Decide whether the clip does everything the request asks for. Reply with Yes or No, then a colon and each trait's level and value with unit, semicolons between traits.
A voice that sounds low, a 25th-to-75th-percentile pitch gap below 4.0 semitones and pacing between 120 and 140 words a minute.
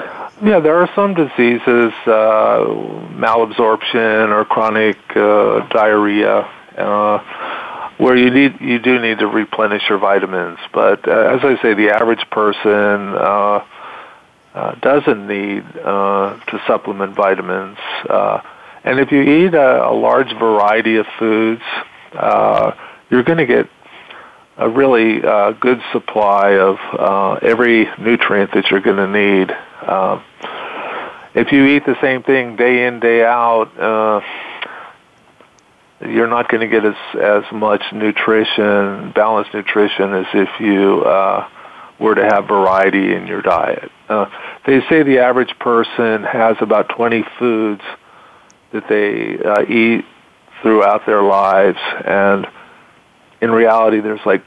Yes: low, 110 Hz; narrow, 2.5 semitones; slow, 135 wpm